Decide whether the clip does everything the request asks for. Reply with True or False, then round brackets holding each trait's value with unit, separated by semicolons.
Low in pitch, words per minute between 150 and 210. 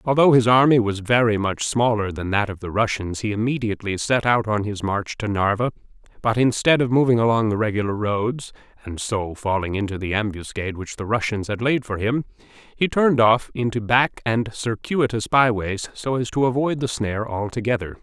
True (110 Hz; 195 wpm)